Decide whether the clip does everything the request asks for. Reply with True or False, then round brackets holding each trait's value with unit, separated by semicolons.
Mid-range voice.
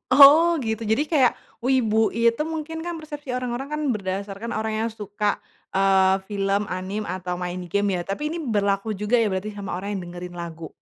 False (210 Hz)